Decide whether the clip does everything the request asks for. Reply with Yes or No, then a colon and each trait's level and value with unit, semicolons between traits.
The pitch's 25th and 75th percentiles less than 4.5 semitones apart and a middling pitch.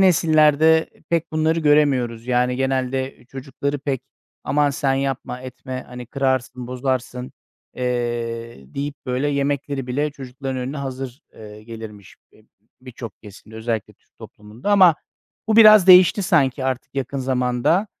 No: average, 2.7 semitones; low, 130 Hz